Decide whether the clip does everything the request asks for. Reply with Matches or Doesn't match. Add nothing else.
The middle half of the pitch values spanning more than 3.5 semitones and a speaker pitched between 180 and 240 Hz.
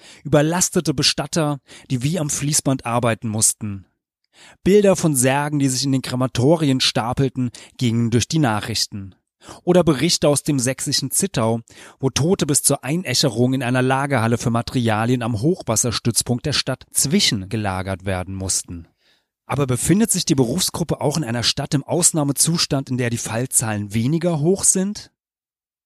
Doesn't match